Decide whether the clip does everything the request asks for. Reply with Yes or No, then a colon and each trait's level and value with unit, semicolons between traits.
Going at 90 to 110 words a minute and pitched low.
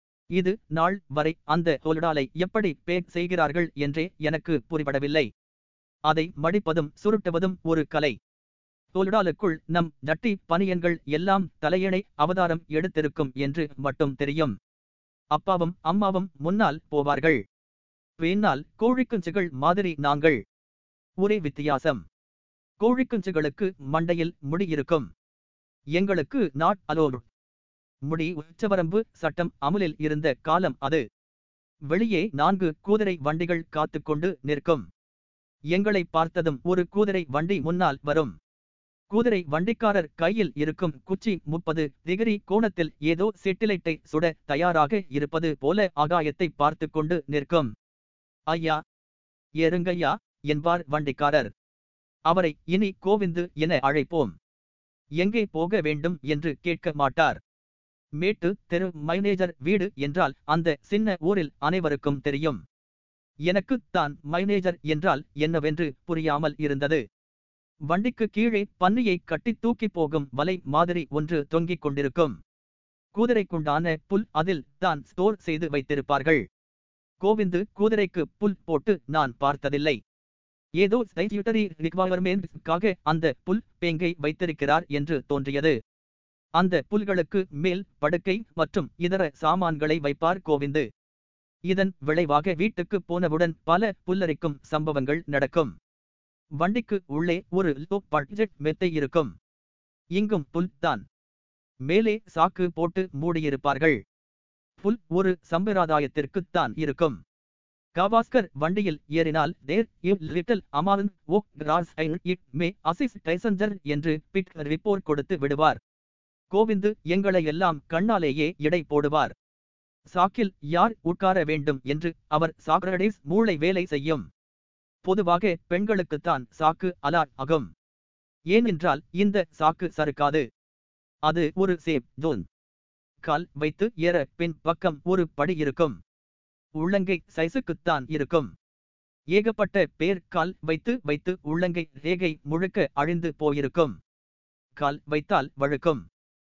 No: average, 100 wpm; medium, 160 Hz